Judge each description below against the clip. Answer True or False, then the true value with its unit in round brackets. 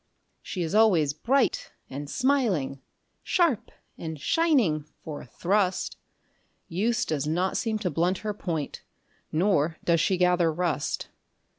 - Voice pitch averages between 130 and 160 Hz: False (180 Hz)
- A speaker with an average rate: False (130 wpm)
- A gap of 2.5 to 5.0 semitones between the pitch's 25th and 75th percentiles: False (5.5 semitones)